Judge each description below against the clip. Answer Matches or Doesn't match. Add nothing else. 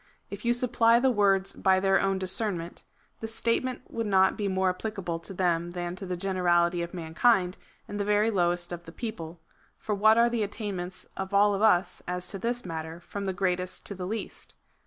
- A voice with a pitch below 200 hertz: Matches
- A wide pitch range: Doesn't match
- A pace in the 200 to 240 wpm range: Matches